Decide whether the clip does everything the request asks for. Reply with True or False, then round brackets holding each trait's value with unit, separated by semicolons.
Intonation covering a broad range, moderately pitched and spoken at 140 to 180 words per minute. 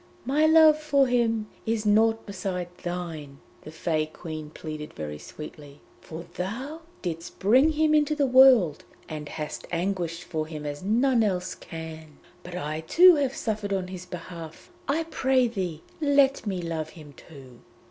True (7.9 semitones; 180 Hz; 160 wpm)